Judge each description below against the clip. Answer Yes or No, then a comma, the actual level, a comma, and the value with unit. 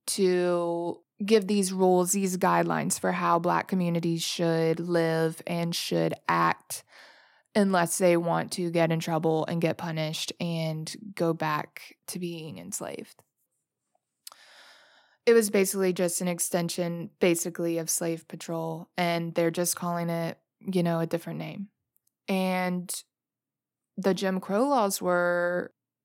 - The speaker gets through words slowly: Yes, slow, 130 wpm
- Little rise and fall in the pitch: Yes, narrow, 1.9 semitones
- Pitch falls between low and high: Yes, medium, 175 Hz